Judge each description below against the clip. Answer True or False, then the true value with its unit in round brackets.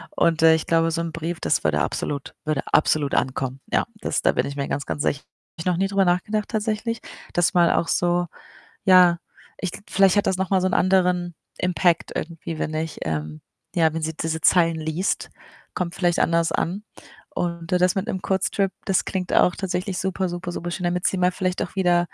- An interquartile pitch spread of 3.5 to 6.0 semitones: False (2.4 semitones)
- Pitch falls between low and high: True (175 Hz)